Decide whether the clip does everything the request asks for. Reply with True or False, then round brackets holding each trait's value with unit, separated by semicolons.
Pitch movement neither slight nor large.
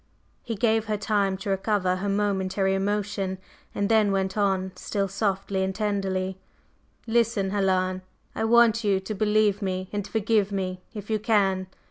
False (1.8 semitones)